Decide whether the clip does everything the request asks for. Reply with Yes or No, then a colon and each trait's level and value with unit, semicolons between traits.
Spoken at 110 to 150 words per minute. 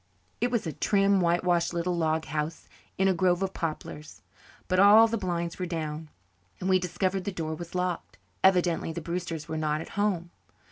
No: average, 190 wpm